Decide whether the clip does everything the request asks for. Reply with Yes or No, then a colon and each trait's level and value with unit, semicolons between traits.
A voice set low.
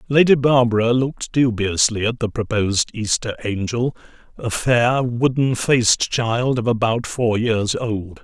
Yes: low, 115 Hz